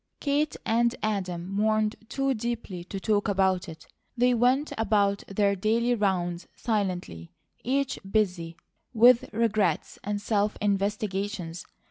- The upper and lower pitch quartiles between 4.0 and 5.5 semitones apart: No, average, 3.3 semitones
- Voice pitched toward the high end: Yes, high, 205 Hz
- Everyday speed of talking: No, slow, 120 wpm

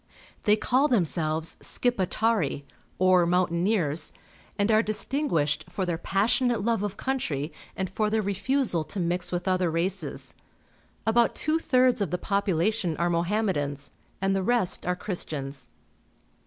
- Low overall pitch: No, high, 190 Hz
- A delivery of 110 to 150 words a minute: Yes, average, 140 wpm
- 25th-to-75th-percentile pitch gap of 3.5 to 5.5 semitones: Yes, average, 4.5 semitones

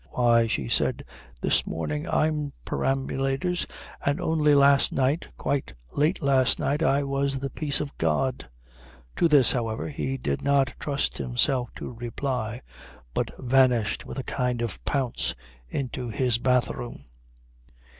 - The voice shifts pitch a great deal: No, average, 2.9 semitones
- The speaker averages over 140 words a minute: No, slow, 135 wpm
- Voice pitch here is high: No, low, 135 Hz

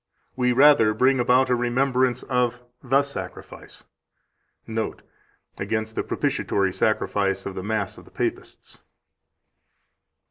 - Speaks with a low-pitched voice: Yes, low, 120 Hz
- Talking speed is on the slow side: Yes, slow, 115 wpm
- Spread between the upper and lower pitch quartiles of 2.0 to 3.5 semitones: Yes, average, 3.1 semitones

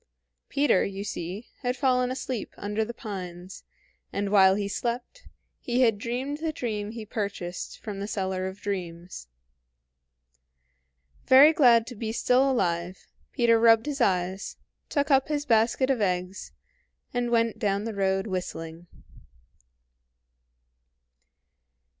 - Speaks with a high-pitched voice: Yes, high, 215 Hz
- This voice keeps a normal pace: No, slow, 130 wpm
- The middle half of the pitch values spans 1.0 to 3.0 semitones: No, average, 4.6 semitones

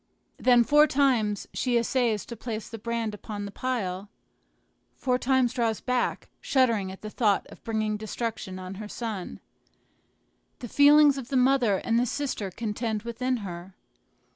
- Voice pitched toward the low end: No, high, 230 Hz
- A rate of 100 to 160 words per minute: Yes, average, 155 wpm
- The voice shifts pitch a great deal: No, average, 3.3 semitones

